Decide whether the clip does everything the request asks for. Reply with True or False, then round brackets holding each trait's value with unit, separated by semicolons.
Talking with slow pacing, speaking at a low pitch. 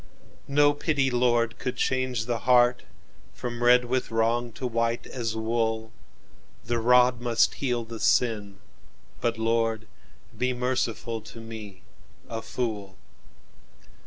True (110 wpm; 120 Hz)